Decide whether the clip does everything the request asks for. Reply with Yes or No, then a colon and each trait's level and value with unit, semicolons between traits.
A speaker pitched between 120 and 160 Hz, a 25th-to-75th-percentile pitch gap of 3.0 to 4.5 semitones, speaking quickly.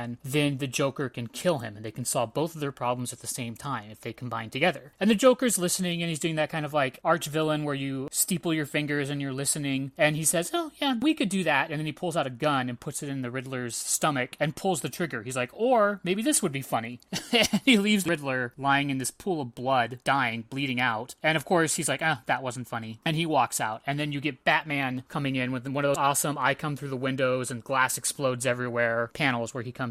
Yes: medium, 140 Hz; average, 4.1 semitones; fast, 260 wpm